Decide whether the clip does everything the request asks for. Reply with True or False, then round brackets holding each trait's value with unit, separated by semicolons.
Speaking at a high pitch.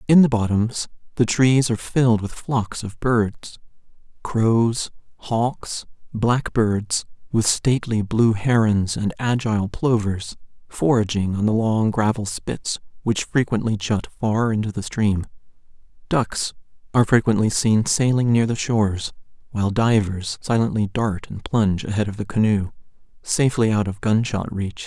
False (110 Hz)